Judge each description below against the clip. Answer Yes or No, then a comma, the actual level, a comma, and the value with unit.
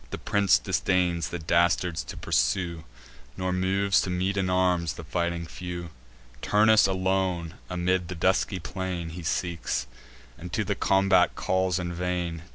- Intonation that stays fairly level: Yes, narrow, 1.5 semitones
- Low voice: Yes, very low, 90 Hz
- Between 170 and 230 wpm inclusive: No, average, 150 wpm